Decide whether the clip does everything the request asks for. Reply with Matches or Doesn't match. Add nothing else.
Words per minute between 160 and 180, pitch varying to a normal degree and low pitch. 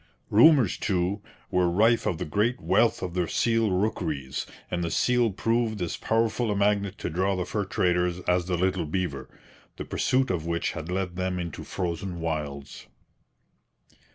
Matches